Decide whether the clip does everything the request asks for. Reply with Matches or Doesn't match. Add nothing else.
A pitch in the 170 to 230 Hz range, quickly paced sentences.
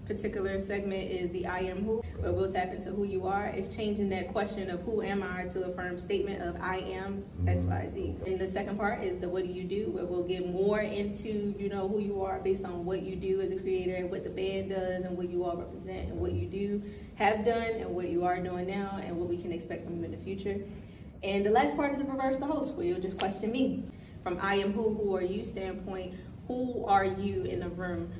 Matches